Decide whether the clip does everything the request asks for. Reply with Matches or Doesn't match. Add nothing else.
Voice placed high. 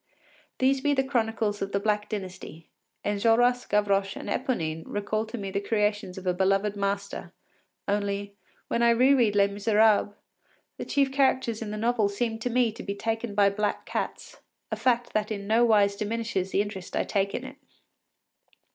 Matches